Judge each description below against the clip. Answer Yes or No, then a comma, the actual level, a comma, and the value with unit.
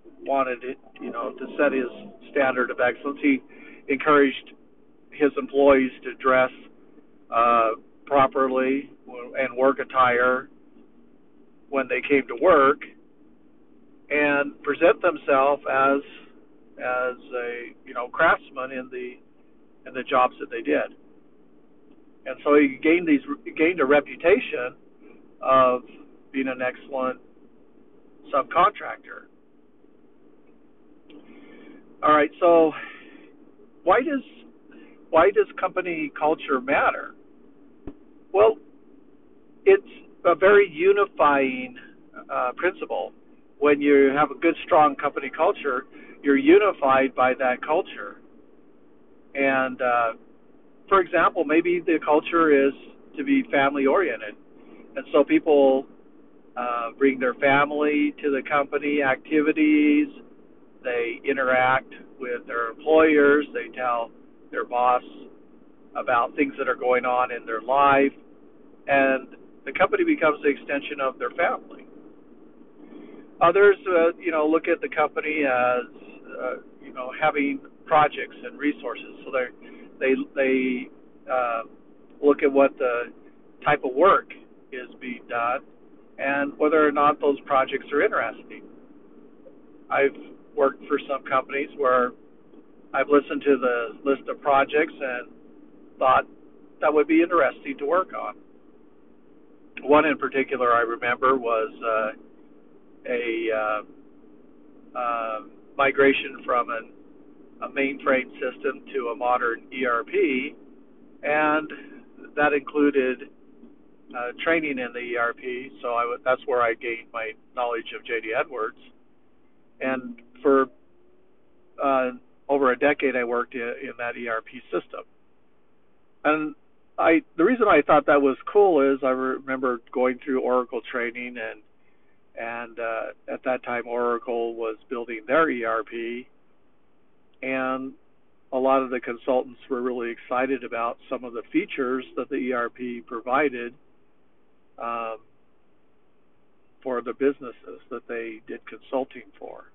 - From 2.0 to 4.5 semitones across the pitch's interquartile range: Yes, average, 2.9 semitones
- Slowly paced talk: Yes, slow, 120 wpm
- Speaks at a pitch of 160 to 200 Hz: No, low, 135 Hz